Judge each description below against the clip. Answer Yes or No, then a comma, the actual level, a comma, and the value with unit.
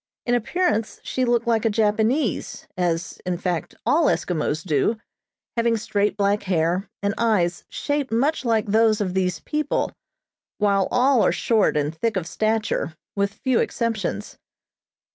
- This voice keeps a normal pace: Yes, average, 145 wpm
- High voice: Yes, high, 210 Hz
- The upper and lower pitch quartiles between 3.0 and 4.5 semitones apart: Yes, average, 4.2 semitones